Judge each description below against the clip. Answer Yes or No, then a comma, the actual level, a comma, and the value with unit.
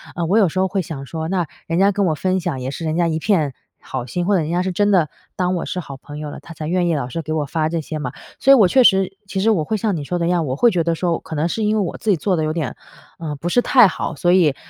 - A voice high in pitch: No, medium, 170 Hz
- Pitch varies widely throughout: No, average, 3.5 semitones